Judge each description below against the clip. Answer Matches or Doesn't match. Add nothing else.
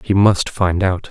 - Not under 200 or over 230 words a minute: Matches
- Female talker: Doesn't match